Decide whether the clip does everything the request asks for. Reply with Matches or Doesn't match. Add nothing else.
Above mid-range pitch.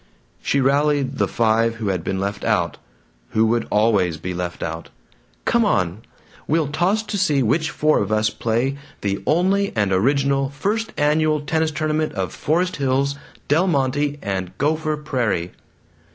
Doesn't match